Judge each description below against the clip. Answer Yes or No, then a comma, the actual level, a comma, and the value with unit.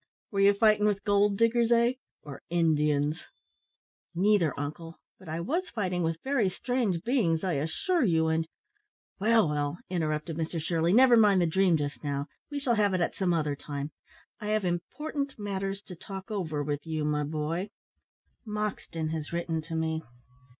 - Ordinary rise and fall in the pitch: Yes, average, 4.9 semitones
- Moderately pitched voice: Yes, medium, 175 Hz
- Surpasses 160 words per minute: Yes, average, 170 wpm